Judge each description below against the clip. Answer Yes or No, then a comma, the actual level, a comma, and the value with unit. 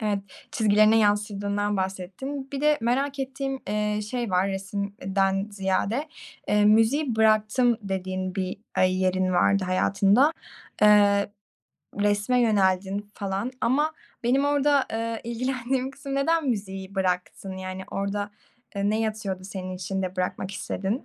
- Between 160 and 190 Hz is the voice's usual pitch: No, high, 205 Hz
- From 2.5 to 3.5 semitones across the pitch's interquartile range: No, average, 4.0 semitones